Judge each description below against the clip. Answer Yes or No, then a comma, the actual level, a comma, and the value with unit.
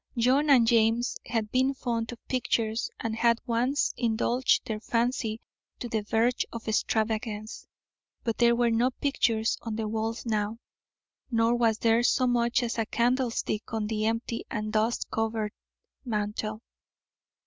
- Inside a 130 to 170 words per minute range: Yes, average, 150 wpm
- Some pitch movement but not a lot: No, narrow, 1.6 semitones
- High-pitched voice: Yes, high, 230 Hz